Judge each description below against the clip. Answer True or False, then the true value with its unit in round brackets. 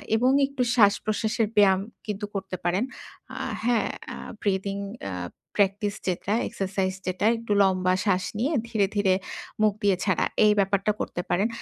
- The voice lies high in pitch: True (200 Hz)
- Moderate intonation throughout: False (2.1 semitones)